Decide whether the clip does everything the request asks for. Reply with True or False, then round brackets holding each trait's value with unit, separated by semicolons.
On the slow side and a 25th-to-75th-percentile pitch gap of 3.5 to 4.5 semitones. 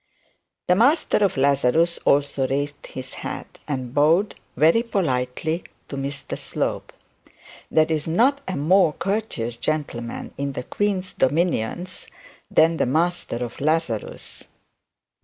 False (120 wpm; 5.0 semitones)